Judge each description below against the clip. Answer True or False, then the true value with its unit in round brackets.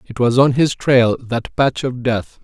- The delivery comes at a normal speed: False (220 wpm)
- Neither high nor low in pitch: False (125 Hz)